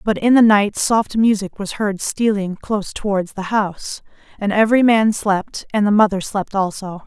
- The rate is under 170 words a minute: No, average, 185 wpm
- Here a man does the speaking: No, female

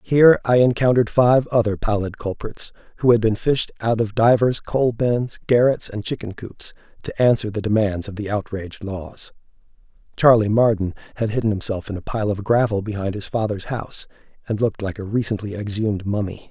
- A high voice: No, low, 110 Hz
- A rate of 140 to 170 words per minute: No, average, 180 wpm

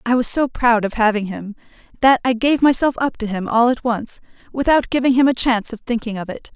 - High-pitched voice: Yes, high, 240 Hz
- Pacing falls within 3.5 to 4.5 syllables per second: No, 5.7 syllables/s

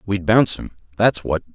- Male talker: Yes, male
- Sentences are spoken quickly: No, average, 195 wpm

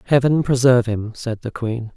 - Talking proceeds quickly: No, average, 185 wpm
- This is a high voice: No, low, 120 Hz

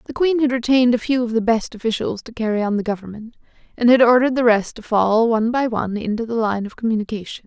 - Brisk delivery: Yes, fast, 240 wpm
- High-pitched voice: Yes, high, 230 Hz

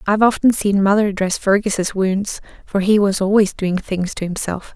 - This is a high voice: Yes, high, 200 Hz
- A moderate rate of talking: Yes, average, 190 wpm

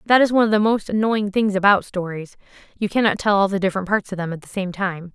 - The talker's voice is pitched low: No, high, 200 Hz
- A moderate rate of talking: No, fast, 270 wpm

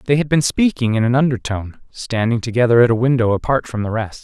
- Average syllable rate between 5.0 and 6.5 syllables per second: Yes, 6.1 syllables/s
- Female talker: No, male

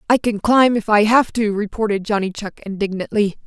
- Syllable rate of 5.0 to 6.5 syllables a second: Yes, 5.3 syllables/s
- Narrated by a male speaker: No, female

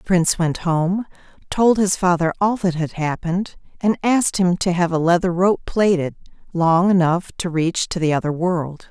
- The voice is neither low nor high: Yes, medium, 175 Hz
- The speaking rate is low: No, average, 190 wpm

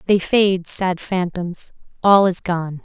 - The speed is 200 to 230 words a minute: No, average, 150 wpm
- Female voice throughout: Yes, female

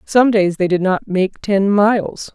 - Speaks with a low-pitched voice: No, high, 200 Hz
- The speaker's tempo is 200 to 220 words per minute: Yes, fast, 205 wpm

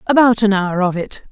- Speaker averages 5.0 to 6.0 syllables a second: Yes, 5.4 syllables/s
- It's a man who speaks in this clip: No, female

